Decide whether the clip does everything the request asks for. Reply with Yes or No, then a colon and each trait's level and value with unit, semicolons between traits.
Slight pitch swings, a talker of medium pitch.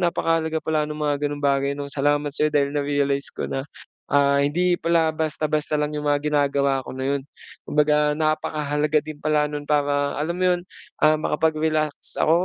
Yes: narrow, 1.4 semitones; medium, 150 Hz